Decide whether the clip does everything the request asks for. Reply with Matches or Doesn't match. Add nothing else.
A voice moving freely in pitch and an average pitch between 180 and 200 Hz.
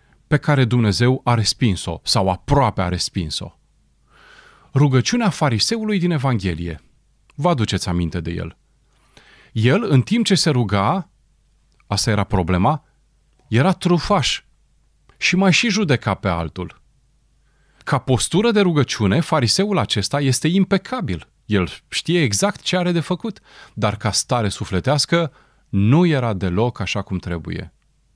Doesn't match